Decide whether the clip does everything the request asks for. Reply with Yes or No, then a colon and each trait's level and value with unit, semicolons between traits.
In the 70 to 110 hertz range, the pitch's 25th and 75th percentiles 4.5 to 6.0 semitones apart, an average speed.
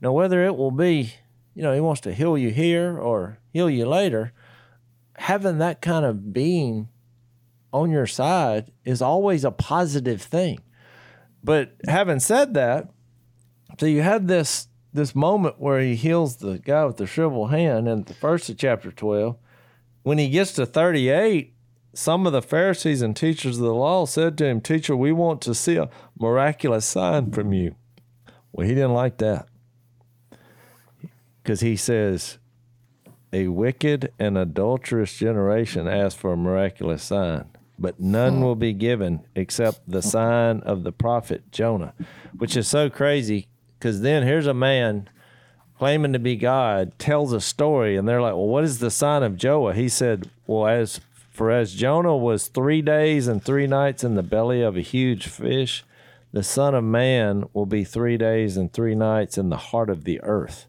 No: low, 120 Hz; average, 4.8 semitones; average, 175 wpm